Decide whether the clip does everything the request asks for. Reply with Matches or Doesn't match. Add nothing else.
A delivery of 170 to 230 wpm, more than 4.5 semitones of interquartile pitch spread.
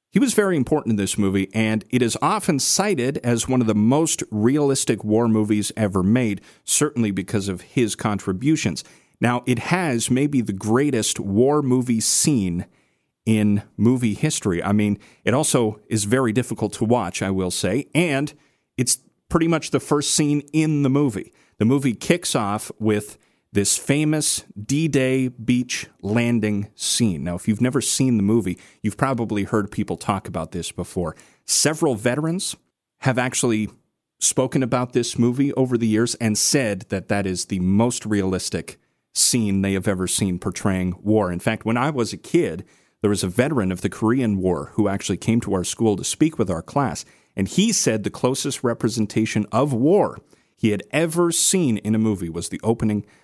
Doesn't match